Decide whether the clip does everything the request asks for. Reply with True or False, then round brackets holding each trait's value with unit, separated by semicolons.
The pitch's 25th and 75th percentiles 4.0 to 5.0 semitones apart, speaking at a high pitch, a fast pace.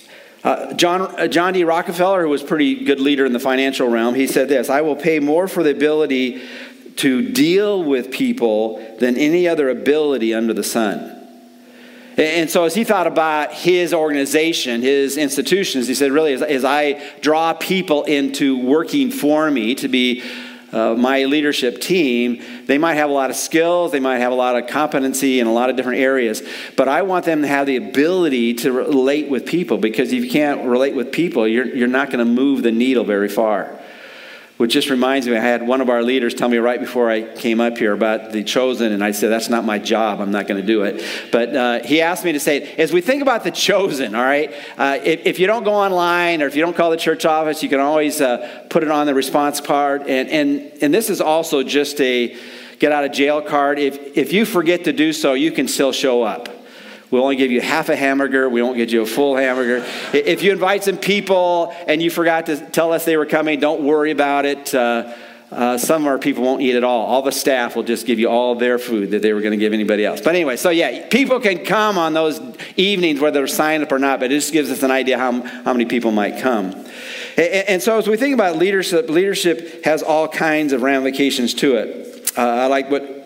False (4.7 semitones; 140 Hz; 235 wpm)